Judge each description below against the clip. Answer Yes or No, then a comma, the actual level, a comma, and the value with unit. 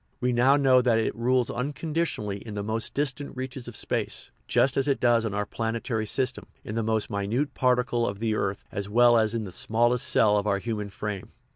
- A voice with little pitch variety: No, average, 3.2 semitones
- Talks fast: Yes, fast, 215 wpm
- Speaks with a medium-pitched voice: No, low, 115 Hz